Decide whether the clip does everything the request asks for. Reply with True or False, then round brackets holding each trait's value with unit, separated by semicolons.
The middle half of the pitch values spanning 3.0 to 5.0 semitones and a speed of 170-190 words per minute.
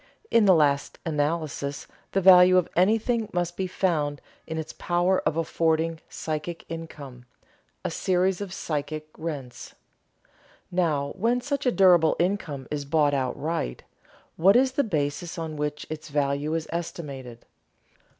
False (3.8 semitones; 140 wpm)